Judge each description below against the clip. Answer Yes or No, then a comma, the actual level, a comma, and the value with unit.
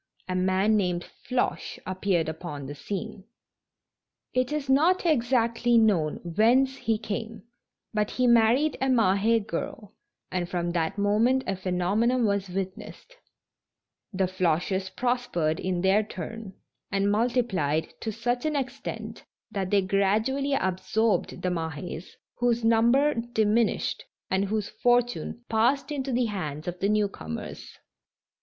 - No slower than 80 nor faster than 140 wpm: Yes, slow, 135 wpm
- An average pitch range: Yes, average, 4.5 semitones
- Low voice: No, high, 210 Hz